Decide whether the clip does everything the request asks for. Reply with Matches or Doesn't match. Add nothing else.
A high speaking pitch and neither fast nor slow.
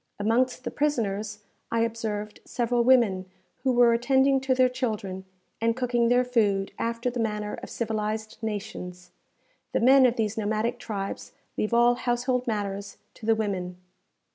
Matches